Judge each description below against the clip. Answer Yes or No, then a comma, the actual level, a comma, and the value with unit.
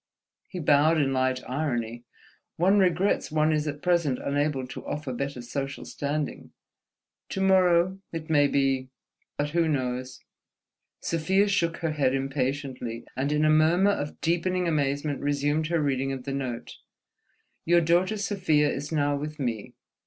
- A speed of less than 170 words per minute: Yes, average, 150 wpm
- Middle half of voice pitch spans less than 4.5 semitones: Yes, average, 3.7 semitones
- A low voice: No, medium, 150 Hz